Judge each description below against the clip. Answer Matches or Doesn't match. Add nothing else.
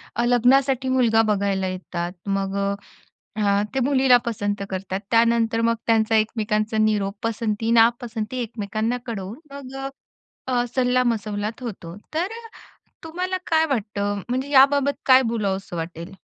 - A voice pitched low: Doesn't match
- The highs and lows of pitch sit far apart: Doesn't match